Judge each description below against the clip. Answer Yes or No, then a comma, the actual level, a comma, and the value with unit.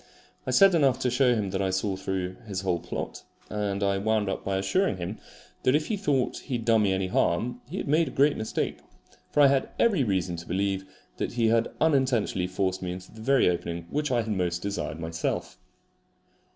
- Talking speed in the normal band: No, fast, 215 wpm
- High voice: No, low, 105 Hz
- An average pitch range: No, wide, 5.7 semitones